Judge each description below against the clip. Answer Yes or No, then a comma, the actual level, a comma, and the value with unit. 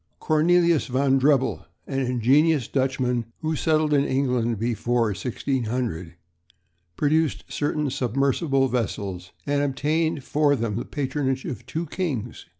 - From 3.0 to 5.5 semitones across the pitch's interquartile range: Yes, average, 3.5 semitones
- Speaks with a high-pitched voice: No, low, 135 Hz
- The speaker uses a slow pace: Yes, slow, 120 wpm